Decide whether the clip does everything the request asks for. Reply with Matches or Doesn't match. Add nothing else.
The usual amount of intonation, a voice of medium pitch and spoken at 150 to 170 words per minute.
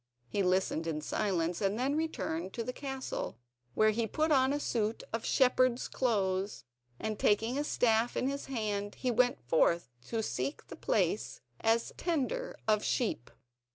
Doesn't match